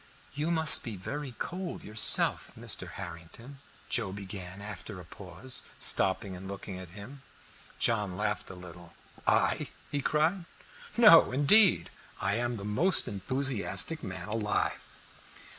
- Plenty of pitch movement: Yes, wide, 6.8 semitones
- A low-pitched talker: Yes, low, 105 Hz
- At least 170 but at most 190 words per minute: No, slow, 135 wpm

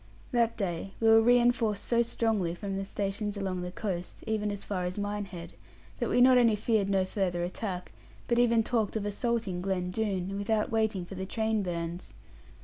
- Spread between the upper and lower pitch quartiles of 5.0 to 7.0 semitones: No, average, 3.2 semitones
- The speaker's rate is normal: Yes, average, 185 wpm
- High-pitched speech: Yes, high, 205 Hz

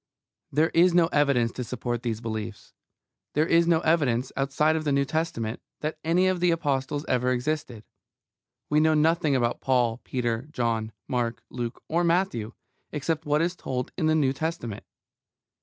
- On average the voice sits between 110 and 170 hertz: Yes, medium, 140 Hz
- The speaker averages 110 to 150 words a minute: No, average, 160 wpm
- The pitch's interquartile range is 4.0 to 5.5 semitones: Yes, average, 4.9 semitones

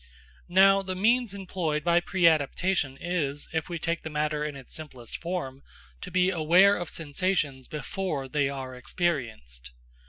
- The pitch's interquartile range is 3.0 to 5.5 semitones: Yes, average, 4.7 semitones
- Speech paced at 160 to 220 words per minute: No, average, 150 wpm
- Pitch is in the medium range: Yes, medium, 160 Hz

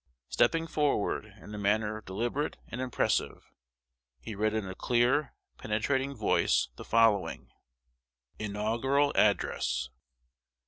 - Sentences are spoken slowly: Yes, slow, 105 wpm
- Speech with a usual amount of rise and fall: Yes, average, 4.2 semitones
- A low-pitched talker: Yes, low, 110 Hz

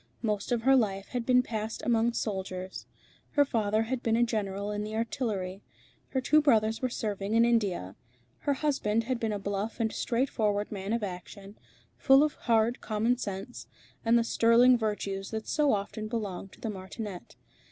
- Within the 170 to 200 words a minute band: Yes, average, 175 wpm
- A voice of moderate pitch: No, high, 220 Hz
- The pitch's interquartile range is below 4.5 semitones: Yes, average, 2.8 semitones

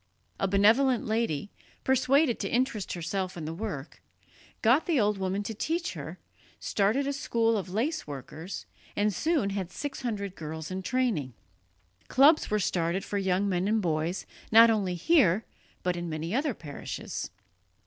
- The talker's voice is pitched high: Yes, high, 205 Hz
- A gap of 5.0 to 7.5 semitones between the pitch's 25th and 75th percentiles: Yes, average, 5.3 semitones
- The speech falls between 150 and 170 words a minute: Yes, average, 160 wpm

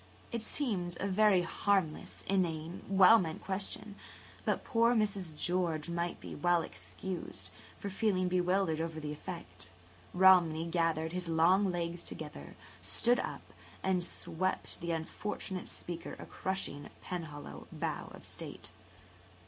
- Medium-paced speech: No, slow, 130 wpm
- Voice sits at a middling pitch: Yes, medium, 175 Hz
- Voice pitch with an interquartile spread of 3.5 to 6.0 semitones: No, average, 2.8 semitones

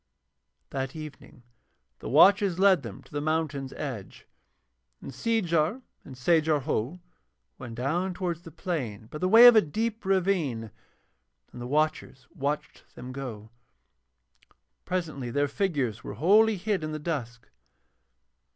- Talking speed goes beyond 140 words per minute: No, slow, 135 wpm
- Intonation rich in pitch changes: Yes, wide, 5.9 semitones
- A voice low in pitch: No, medium, 155 Hz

